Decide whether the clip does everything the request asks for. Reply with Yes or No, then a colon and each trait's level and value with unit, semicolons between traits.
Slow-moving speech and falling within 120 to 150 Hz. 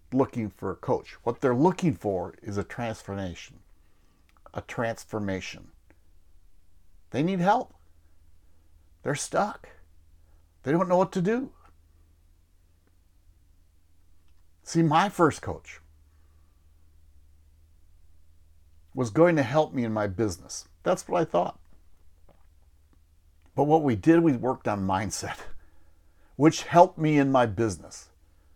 No: slow, 115 wpm; very low, 80 Hz